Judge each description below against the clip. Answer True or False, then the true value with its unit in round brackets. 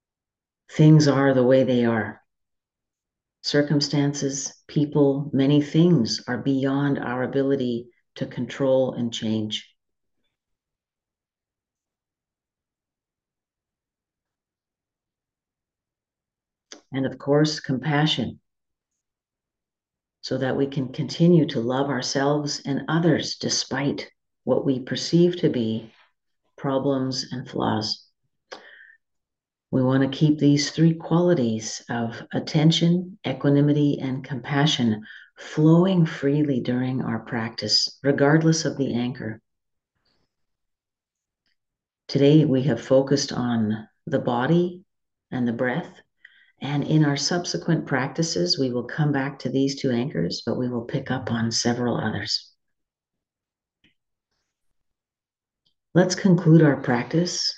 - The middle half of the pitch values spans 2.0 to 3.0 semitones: False (3.5 semitones)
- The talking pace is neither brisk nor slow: False (100 wpm)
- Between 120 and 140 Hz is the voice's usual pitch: True (135 Hz)